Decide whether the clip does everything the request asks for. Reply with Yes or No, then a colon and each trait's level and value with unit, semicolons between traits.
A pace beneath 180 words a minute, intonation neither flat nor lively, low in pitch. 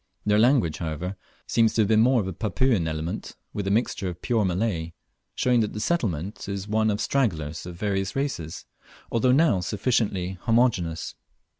Yes: average, 165 wpm; average, 4.6 semitones; low, 105 Hz